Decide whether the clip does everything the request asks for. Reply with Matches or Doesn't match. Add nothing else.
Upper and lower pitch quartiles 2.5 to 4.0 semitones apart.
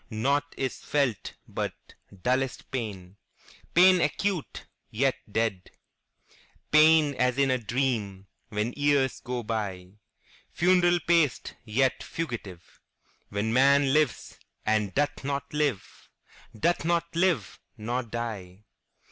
Doesn't match